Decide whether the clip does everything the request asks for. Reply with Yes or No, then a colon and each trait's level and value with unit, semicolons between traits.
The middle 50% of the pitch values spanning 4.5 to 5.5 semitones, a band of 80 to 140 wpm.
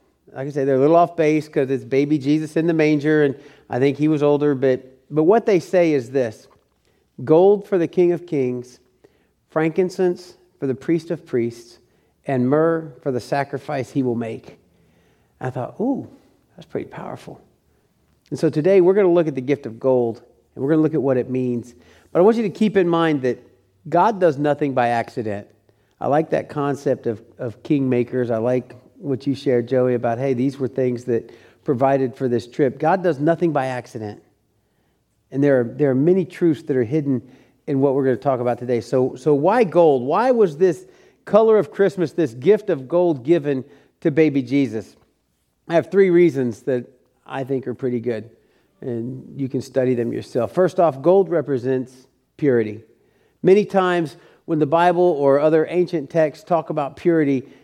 No: average, 4.8 semitones; average, 195 wpm